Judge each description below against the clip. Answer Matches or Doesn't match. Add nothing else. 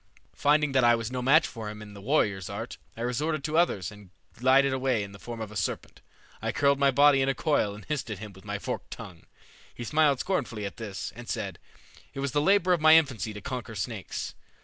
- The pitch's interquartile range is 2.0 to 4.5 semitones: Doesn't match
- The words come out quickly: Matches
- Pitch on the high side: Doesn't match